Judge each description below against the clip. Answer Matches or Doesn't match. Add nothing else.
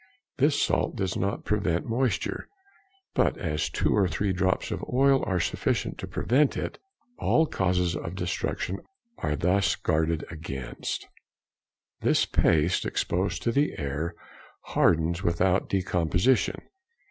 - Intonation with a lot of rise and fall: Doesn't match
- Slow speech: Matches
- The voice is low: Matches